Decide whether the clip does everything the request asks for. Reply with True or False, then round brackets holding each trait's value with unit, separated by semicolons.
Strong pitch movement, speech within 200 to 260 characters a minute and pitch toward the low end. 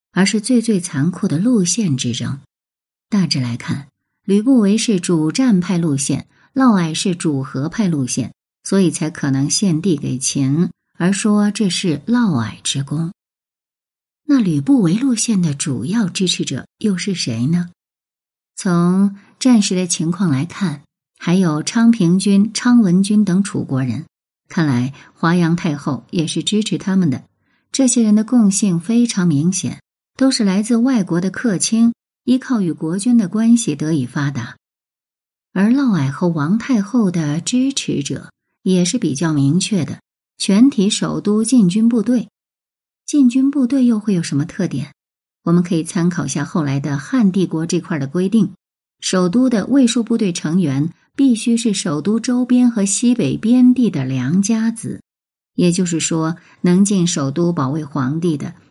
False (5.9 semitones; 230 characters per minute; 185 Hz)